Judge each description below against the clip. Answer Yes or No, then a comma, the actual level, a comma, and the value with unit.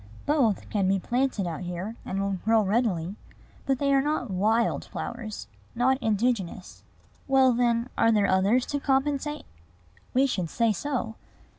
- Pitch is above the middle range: Yes, high, 230 Hz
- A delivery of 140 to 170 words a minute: Yes, average, 150 wpm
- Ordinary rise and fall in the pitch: Yes, average, 5.0 semitones